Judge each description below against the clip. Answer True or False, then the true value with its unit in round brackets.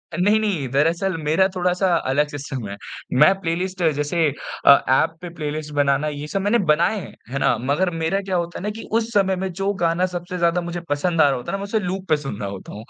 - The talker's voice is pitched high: False (170 Hz)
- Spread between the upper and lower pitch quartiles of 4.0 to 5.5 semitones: True (4.3 semitones)